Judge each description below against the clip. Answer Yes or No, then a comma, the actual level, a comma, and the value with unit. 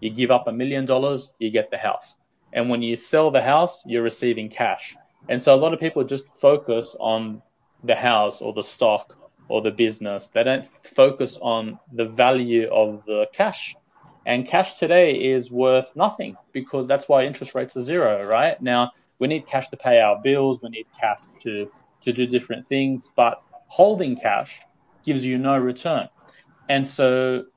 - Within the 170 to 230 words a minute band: Yes, average, 185 wpm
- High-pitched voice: No, low, 130 Hz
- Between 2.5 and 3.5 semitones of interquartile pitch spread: Yes, average, 2.8 semitones